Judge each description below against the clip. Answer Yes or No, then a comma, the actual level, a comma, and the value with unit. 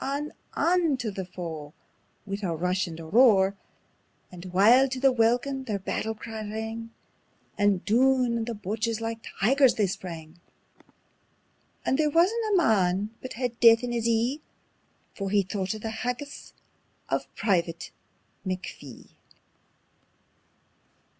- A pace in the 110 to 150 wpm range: Yes, average, 140 wpm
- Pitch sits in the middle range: No, high, 225 Hz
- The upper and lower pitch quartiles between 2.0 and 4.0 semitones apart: No, average, 4.7 semitones